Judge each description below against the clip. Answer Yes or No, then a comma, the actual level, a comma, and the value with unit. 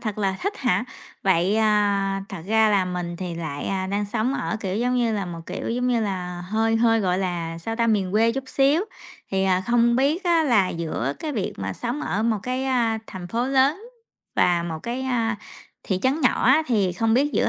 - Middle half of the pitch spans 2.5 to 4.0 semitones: No, average, 4.7 semitones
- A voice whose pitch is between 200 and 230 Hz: Yes, high, 215 Hz